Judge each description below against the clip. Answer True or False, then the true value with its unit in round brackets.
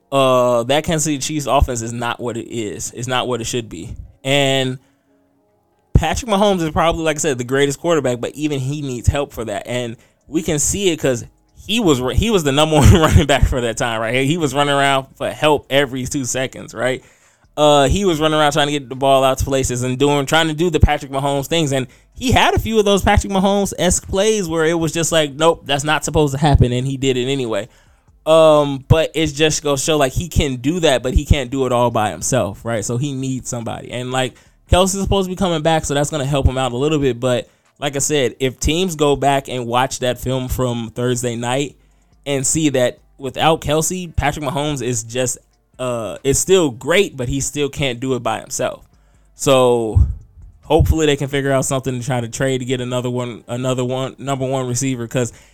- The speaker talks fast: True (230 wpm)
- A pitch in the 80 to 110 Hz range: False (135 Hz)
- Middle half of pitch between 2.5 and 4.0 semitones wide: True (3.4 semitones)